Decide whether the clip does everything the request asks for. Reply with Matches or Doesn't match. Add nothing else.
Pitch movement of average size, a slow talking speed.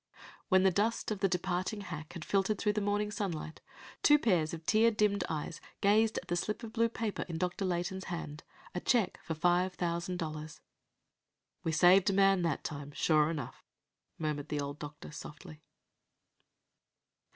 Doesn't match